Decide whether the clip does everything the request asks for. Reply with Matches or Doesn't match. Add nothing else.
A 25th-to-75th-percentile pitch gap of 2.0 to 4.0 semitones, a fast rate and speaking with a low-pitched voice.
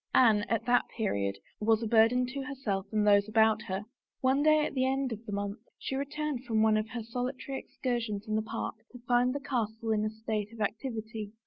Doesn't match